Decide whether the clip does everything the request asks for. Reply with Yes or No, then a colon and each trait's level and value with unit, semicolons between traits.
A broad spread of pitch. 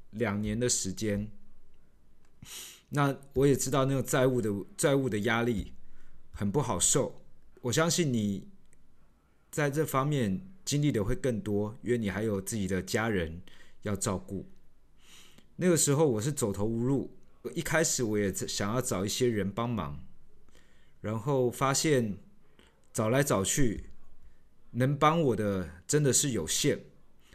Yes: wide, 5.8 semitones